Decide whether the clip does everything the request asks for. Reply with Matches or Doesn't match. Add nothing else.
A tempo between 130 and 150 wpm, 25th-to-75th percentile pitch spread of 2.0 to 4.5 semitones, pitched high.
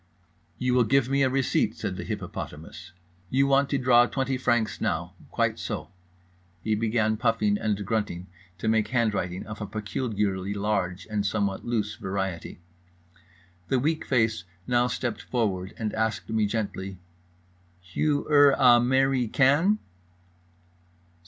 Doesn't match